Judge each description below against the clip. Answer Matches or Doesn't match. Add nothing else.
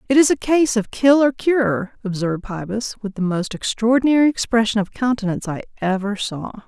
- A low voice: Doesn't match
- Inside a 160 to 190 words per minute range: Matches